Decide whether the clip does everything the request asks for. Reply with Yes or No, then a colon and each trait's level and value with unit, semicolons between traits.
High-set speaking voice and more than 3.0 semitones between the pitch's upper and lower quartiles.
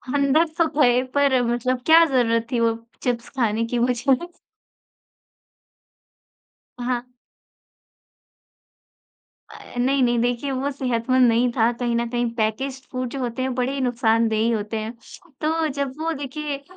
No: very high, 250 Hz; narrow, 2.5 semitones